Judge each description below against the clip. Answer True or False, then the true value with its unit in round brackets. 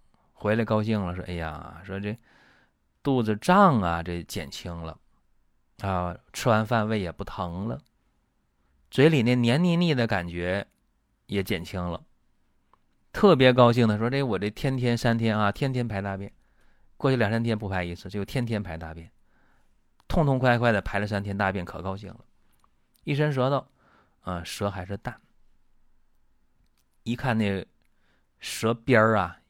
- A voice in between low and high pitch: False (105 Hz)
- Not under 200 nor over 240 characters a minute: True (215 characters per minute)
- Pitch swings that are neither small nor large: True (5.0 semitones)